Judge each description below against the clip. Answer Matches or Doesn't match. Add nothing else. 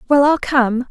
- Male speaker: Doesn't match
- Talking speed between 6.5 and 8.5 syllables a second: Doesn't match